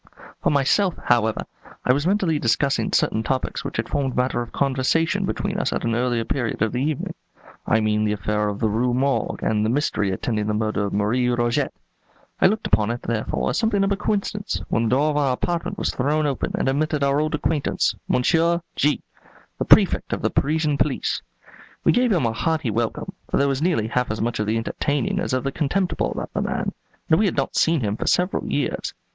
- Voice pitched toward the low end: Yes, low, 130 Hz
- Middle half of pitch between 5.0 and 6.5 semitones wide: Yes, wide, 5.5 semitones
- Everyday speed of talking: No, fast, 215 wpm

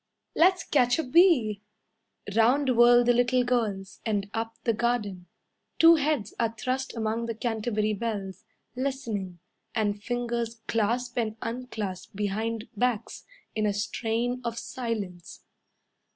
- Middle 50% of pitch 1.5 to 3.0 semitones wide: Yes, narrow, 2.6 semitones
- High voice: Yes, high, 230 Hz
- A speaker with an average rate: No, slow, 125 wpm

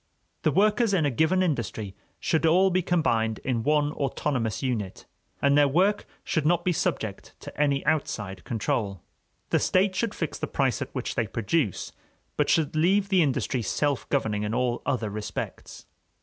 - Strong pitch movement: Yes, wide, 7.1 semitones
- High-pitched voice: No, medium, 140 Hz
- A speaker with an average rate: Yes, average, 170 wpm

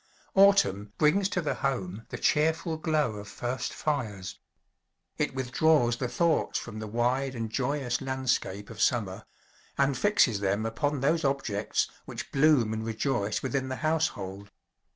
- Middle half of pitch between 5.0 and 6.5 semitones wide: Yes, wide, 5.6 semitones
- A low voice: Yes, low, 130 Hz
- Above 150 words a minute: No, average, 145 wpm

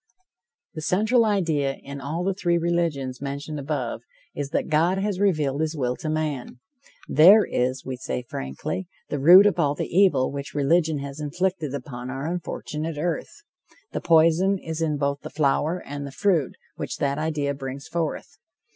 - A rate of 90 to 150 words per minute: No, average, 170 wpm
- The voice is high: No, medium, 155 Hz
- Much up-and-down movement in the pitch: No, average, 3.7 semitones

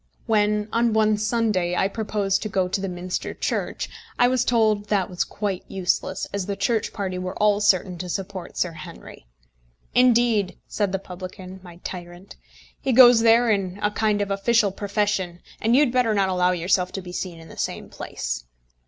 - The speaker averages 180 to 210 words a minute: Yes, average, 190 wpm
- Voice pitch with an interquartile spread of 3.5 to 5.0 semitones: No, average, 2.9 semitones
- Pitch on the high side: Yes, high, 200 Hz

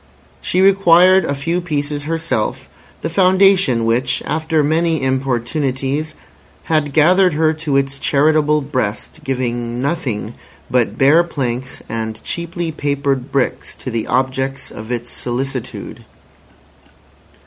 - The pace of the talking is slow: Yes, slow, 115 wpm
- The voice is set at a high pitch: No, medium, 140 Hz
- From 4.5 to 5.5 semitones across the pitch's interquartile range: No, average, 4.0 semitones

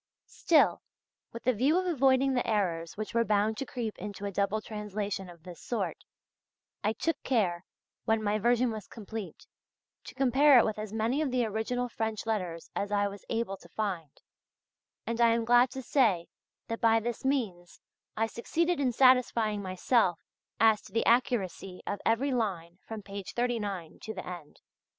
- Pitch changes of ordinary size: Yes, average, 3.5 semitones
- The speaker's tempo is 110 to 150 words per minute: No, average, 175 wpm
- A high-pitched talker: Yes, high, 220 Hz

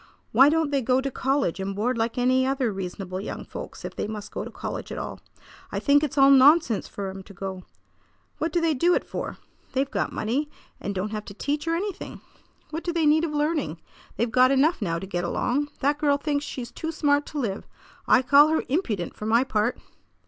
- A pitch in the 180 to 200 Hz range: No, very high, 265 Hz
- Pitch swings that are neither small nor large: No, wide, 5.8 semitones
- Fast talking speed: Yes, fast, 220 wpm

